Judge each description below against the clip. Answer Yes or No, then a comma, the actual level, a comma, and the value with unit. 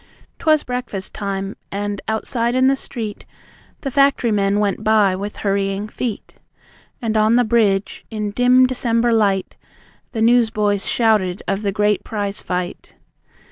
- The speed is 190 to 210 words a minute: No, average, 140 wpm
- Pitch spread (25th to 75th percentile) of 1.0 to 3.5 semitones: Yes, average, 2.9 semitones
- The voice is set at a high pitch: Yes, high, 215 Hz